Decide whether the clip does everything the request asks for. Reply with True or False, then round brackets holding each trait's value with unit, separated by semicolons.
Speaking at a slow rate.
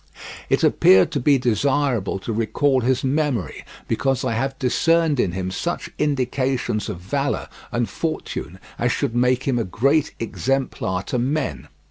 False (150 wpm)